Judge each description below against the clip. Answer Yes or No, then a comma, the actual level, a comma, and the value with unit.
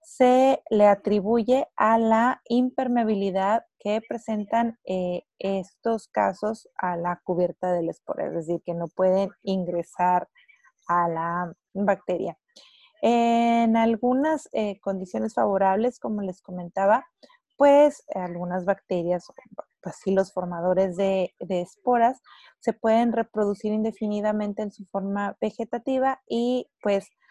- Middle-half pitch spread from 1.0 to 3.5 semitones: No, average, 4.2 semitones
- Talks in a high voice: Yes, high, 205 Hz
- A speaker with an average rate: No, slow, 115 wpm